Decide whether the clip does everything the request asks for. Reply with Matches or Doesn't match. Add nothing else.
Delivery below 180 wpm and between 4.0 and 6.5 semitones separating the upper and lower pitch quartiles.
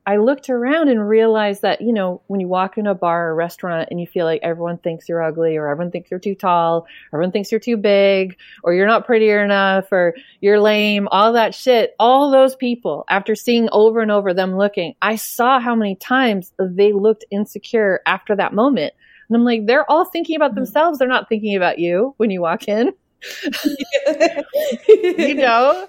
Doesn't match